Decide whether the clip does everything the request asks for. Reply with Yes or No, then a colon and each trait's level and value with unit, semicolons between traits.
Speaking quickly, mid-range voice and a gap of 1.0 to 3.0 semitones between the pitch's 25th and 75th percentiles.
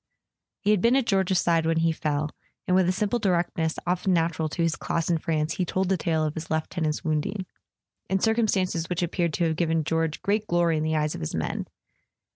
Yes: fast, 230 wpm; medium, 170 Hz; average, 2.7 semitones